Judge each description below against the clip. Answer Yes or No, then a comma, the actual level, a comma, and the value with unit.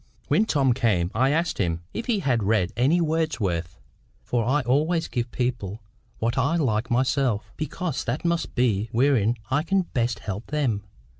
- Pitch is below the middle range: Yes, low, 125 Hz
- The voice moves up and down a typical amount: No, wide, 5.8 semitones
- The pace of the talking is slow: No, average, 170 wpm